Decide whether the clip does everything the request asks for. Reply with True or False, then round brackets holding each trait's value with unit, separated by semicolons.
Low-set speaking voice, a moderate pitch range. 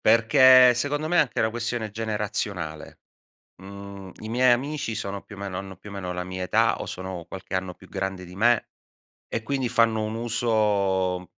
True (105 Hz; 3.7 semitones)